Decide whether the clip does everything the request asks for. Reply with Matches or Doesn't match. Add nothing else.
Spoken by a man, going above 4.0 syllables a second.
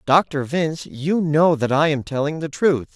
Matches